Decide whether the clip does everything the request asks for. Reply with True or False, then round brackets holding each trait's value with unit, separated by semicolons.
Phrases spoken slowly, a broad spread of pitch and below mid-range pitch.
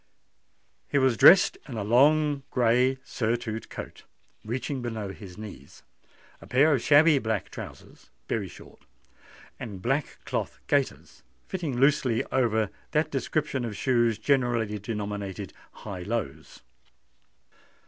False (120 wpm; 4.2 semitones; 120 Hz)